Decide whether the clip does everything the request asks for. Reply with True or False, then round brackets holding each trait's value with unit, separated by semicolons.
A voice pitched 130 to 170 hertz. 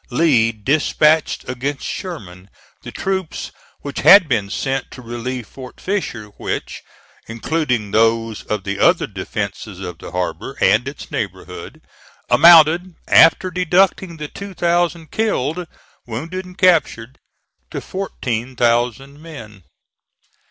True (135 Hz)